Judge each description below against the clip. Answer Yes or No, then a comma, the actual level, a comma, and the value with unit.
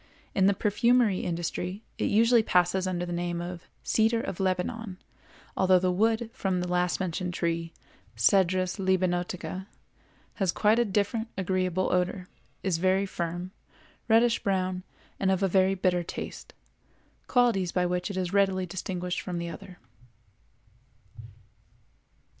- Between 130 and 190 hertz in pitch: Yes, medium, 185 Hz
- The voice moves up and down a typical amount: No, narrow, 1.8 semitones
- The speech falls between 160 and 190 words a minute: No, slow, 135 wpm